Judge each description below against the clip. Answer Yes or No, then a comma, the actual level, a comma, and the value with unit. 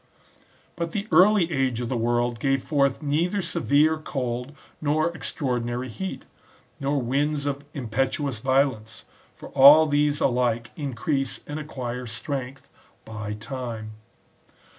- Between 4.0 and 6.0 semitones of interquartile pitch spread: No, average, 3.6 semitones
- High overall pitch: No, low, 135 Hz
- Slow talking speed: Yes, slow, 120 wpm